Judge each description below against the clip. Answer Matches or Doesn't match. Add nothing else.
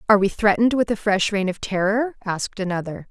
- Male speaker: Doesn't match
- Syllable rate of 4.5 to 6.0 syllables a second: Doesn't match